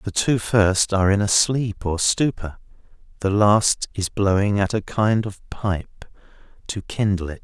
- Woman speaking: No, male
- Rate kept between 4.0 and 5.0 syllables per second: Yes, 4.1 syllables/s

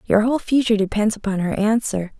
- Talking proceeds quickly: No, average, 190 wpm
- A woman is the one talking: Yes, female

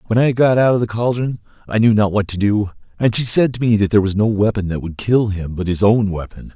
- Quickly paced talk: Yes, fast, 285 wpm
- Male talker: Yes, male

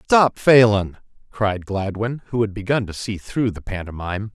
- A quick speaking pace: No, average, 165 wpm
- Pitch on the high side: No, low, 105 Hz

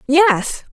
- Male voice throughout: No, female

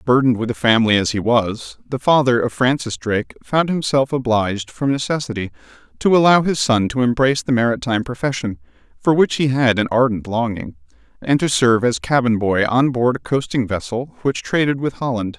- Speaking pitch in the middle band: No, low, 125 Hz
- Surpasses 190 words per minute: No, average, 185 wpm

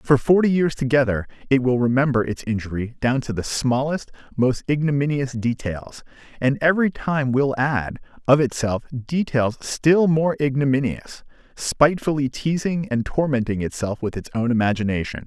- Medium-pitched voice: No, low, 130 Hz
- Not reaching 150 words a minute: Yes, average, 140 wpm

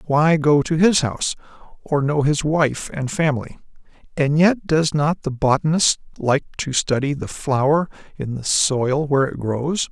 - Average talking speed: Yes, average, 170 wpm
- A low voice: No, medium, 145 Hz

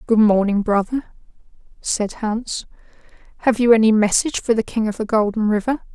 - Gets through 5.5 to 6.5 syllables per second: No, 5.3 syllables/s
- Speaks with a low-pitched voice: No, high, 220 Hz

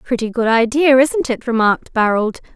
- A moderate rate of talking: Yes, average, 165 wpm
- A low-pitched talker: No, high, 240 Hz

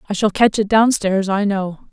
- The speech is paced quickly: Yes, fast, 250 wpm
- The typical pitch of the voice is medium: No, high, 205 Hz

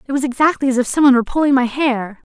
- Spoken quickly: Yes, fast, 260 wpm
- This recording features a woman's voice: Yes, female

